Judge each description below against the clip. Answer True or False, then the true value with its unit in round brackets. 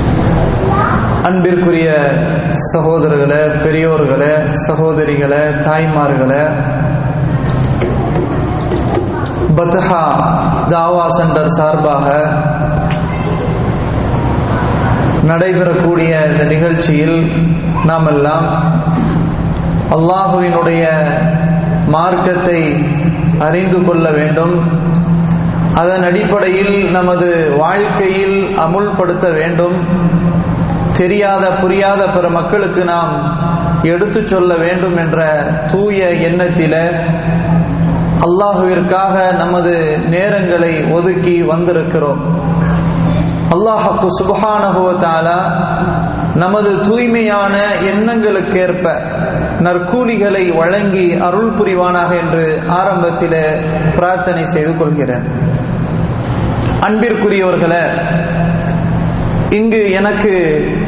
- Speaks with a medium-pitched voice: True (170 Hz)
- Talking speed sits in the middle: False (55 wpm)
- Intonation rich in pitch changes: False (2.5 semitones)